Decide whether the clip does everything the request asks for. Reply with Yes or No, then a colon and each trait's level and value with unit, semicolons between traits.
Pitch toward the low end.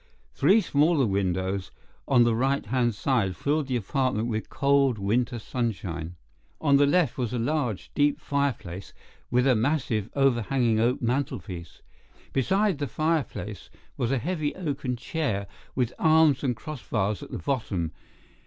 Yes: low, 125 Hz